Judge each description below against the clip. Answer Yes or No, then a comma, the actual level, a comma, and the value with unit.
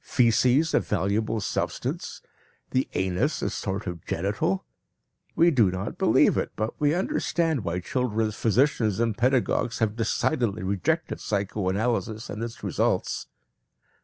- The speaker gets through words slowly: Yes, slow, 130 wpm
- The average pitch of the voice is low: Yes, low, 110 Hz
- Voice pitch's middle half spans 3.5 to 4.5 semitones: Yes, average, 4.2 semitones